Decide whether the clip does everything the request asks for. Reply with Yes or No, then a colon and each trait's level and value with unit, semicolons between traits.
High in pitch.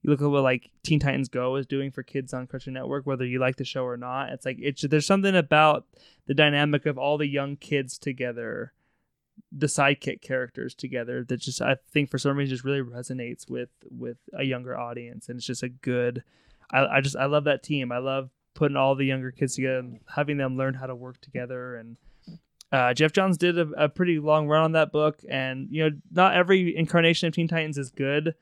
No: low, 135 Hz